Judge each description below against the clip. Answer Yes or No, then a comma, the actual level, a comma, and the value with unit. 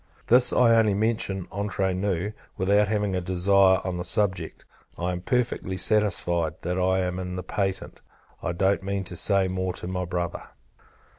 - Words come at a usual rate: Yes, average, 170 wpm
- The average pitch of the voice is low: Yes, very low, 95 Hz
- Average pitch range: No, narrow, 2.0 semitones